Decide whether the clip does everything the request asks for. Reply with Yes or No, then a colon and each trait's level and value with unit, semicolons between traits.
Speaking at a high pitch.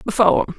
Yes: high, 215 Hz